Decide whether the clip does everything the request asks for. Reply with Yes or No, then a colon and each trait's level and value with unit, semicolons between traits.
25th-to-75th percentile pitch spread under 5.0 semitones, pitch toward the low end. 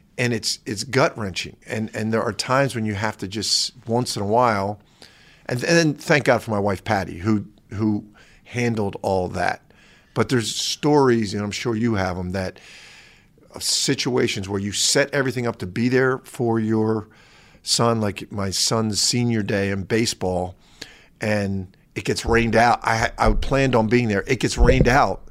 Yes: average, 3.0 semitones; low, 110 Hz